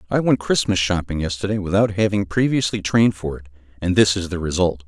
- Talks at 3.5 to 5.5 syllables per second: No, 6.0 syllables/s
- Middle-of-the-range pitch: No, very low, 95 Hz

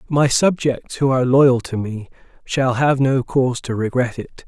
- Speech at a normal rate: Yes, average, 190 wpm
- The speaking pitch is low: Yes, low, 130 Hz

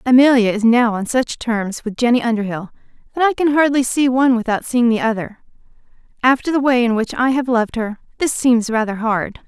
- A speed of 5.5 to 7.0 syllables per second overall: Yes, 5.6 syllables/s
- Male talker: No, female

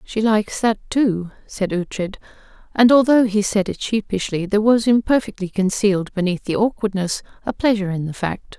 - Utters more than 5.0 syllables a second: Yes, 5.4 syllables/s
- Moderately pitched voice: No, high, 205 Hz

